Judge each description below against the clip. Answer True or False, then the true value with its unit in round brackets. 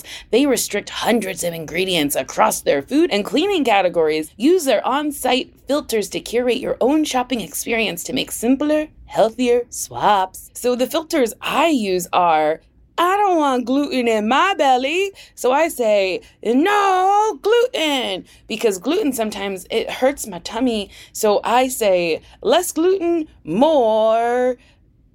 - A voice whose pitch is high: True (250 Hz)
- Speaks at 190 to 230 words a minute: False (135 wpm)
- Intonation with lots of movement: True (6.6 semitones)